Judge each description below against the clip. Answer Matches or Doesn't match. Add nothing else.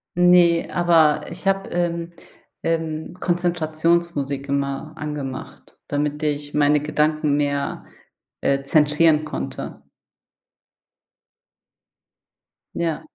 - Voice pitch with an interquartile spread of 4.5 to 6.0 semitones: Doesn't match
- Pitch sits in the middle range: Matches